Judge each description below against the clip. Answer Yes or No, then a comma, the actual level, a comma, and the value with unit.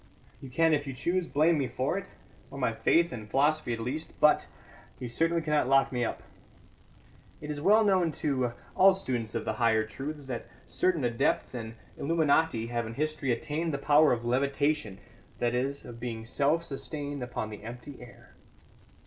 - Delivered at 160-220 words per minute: Yes, average, 180 wpm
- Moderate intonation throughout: Yes, average, 4.5 semitones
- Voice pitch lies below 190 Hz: Yes, medium, 140 Hz